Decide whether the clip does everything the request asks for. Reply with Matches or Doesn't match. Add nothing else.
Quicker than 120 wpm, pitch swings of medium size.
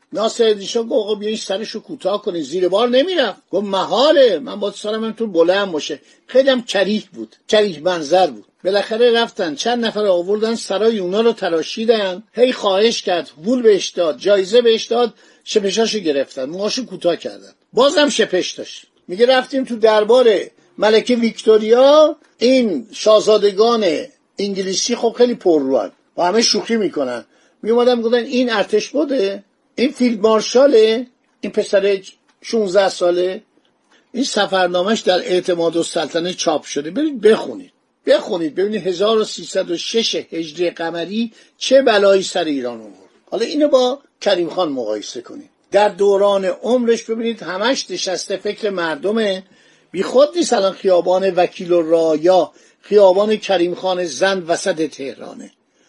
Matches